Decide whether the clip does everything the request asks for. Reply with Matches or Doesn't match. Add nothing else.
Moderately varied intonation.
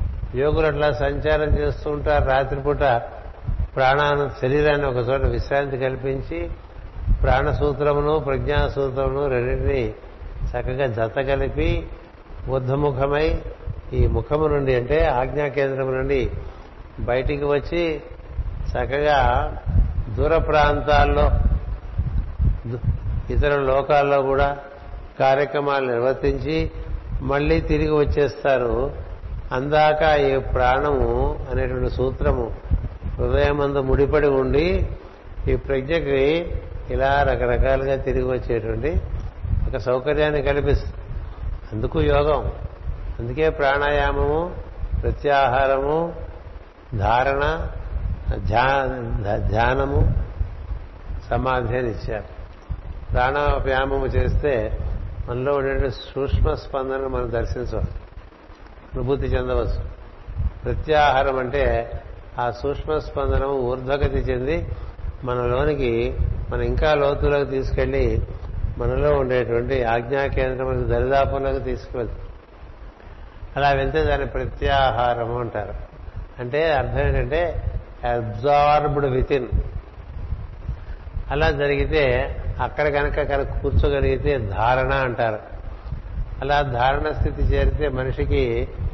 Doesn't match